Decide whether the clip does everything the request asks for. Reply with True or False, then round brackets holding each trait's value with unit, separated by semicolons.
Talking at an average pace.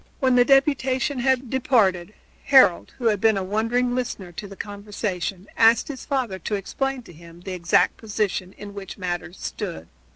True (170 wpm)